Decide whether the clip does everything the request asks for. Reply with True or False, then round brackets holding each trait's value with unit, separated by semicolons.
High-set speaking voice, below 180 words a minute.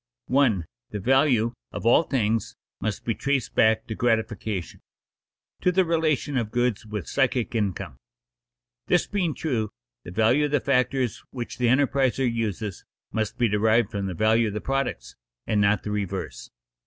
False (115 Hz; 160 wpm)